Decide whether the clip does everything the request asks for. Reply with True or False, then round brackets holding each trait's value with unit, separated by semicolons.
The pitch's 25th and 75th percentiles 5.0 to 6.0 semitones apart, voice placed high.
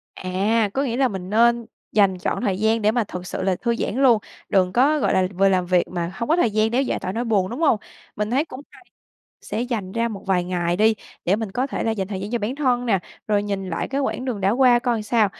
False (4.1 semitones; 215 Hz)